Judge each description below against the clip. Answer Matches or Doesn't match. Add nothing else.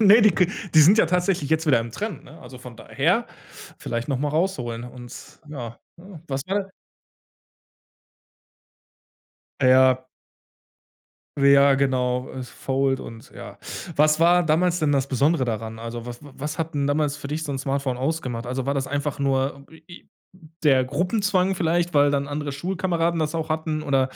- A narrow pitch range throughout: Doesn't match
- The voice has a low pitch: Doesn't match